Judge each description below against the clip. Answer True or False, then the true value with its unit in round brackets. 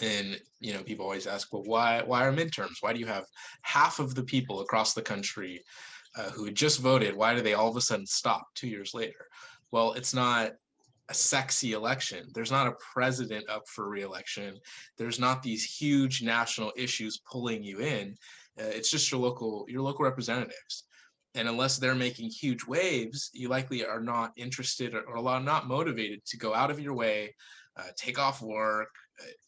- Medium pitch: False (120 Hz)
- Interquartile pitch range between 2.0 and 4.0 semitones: True (3.1 semitones)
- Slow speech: False (190 wpm)